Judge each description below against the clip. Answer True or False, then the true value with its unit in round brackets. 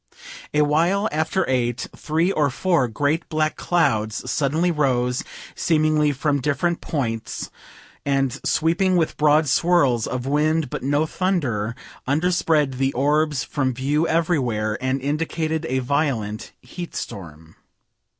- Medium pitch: True (145 Hz)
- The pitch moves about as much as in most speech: True (3.9 semitones)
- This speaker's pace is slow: True (120 wpm)